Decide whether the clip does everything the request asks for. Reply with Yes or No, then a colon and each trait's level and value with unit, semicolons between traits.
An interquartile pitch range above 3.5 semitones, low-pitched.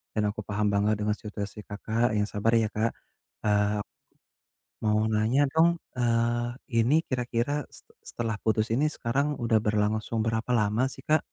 No: narrow, 2.4 semitones; low, 115 Hz